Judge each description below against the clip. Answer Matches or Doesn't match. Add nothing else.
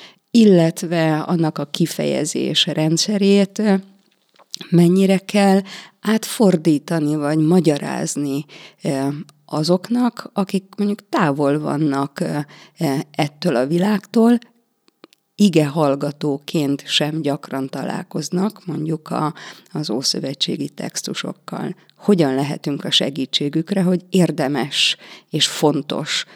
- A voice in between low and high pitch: Matches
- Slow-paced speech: Matches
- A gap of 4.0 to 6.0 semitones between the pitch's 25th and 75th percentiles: Matches